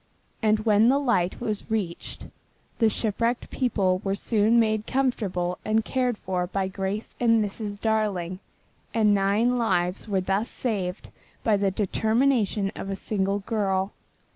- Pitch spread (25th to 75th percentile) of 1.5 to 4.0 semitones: Yes, average, 2.7 semitones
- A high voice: Yes, high, 210 Hz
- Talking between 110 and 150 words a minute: Yes, average, 140 wpm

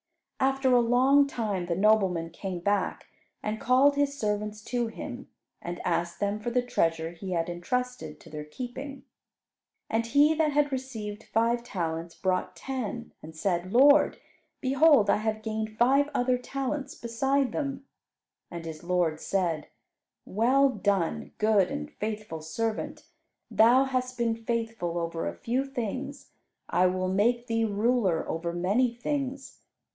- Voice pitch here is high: Yes, high, 225 Hz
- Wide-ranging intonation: Yes, wide, 5.9 semitones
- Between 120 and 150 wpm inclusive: Yes, average, 145 wpm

